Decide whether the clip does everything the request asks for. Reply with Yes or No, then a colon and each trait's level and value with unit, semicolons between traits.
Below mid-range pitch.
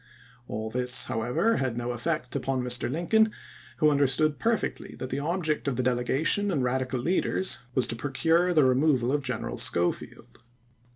Yes: low, 130 Hz